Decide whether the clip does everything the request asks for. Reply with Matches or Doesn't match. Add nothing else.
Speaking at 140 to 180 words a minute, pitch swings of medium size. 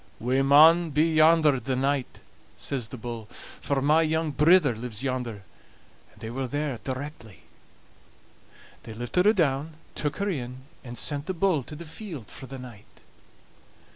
Matches